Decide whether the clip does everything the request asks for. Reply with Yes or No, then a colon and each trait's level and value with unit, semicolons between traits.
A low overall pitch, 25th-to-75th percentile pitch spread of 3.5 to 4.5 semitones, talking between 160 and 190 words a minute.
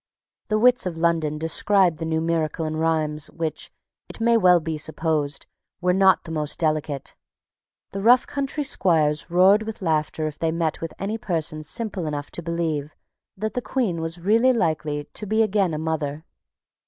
No: medium, 165 Hz; average, 4.1 semitones; average, 175 wpm